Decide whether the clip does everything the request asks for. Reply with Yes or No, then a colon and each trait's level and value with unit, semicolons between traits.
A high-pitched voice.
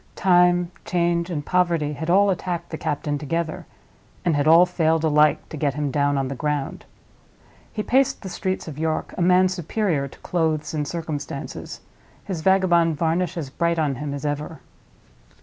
No: medium, 160 Hz